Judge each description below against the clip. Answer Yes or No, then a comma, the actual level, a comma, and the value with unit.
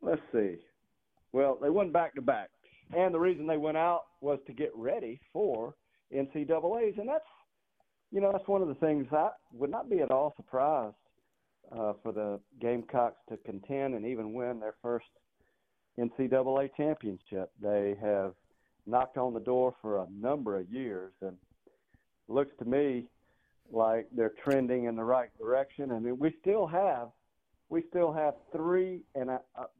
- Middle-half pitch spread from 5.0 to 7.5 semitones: Yes, wide, 5.5 semitones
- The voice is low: Yes, low, 130 Hz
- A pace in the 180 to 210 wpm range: No, average, 170 wpm